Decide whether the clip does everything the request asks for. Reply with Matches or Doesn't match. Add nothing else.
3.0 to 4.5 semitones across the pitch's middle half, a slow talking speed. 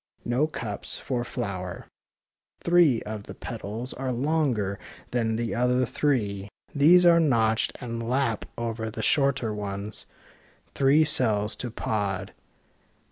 Matches